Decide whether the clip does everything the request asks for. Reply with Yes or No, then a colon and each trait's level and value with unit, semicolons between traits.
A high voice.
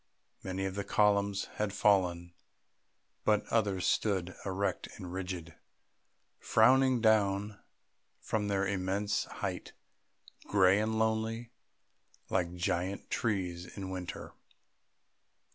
No: low, 100 Hz